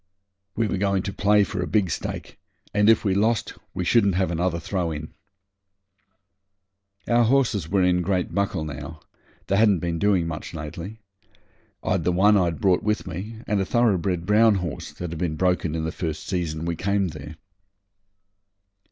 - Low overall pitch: Yes, very low, 95 Hz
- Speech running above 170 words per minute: Yes, average, 180 wpm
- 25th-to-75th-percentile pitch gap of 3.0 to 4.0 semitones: Yes, average, 3.4 semitones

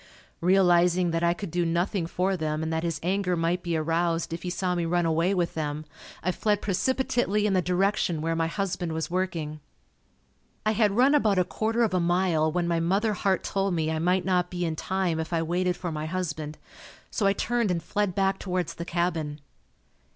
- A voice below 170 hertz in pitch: No, medium, 175 Hz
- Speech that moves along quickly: Yes, fast, 210 wpm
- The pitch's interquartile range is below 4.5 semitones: Yes, average, 2.7 semitones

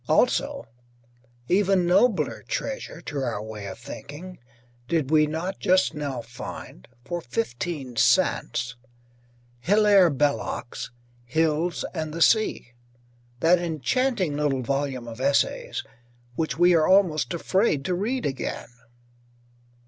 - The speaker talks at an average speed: No, slow, 115 wpm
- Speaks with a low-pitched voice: No, medium, 155 Hz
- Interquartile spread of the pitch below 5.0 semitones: No, wide, 5.5 semitones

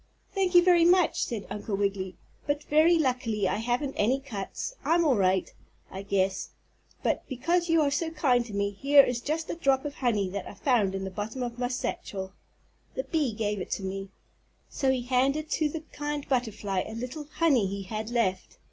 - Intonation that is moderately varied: No, wide, 6.6 semitones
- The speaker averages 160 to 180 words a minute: No, average, 200 wpm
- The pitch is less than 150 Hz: No, high, 245 Hz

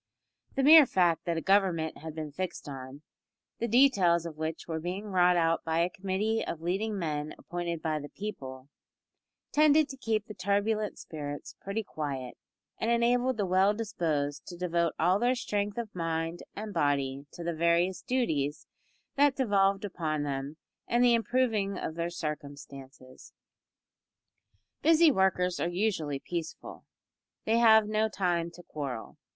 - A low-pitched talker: No, medium, 180 Hz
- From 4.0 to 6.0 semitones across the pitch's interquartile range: Yes, average, 5.3 semitones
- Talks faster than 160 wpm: No, average, 155 wpm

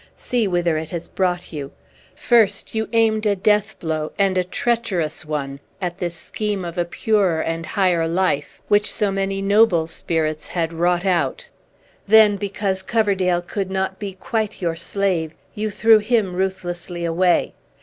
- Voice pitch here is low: No, medium, 185 Hz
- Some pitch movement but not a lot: Yes, average, 3.4 semitones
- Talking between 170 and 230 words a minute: No, average, 160 wpm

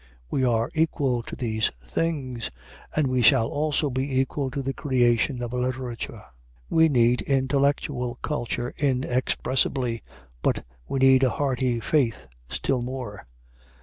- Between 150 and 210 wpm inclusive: No, slow, 135 wpm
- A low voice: Yes, low, 130 Hz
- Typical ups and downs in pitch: No, narrow, 2.3 semitones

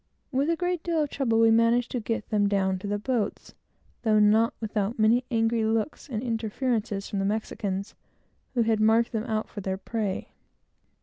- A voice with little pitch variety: Yes, narrow, 2.3 semitones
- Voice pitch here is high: Yes, high, 225 Hz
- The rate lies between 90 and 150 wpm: No, average, 185 wpm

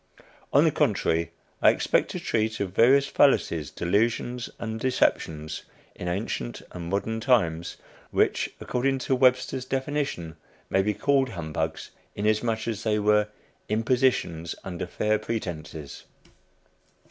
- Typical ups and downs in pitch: No, wide, 6.4 semitones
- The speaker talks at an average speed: No, slow, 125 wpm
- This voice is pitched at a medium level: No, low, 105 Hz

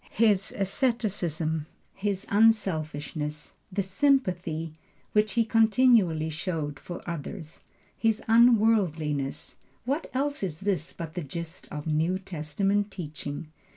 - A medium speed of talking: No, slow, 110 wpm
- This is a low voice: No, medium, 185 Hz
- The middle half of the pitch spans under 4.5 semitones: No, wide, 5.5 semitones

